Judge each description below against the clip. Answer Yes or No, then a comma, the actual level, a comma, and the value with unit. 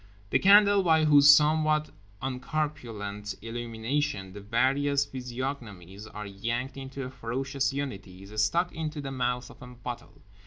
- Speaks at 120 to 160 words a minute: Yes, average, 140 wpm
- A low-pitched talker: Yes, low, 130 Hz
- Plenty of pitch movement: No, average, 4.5 semitones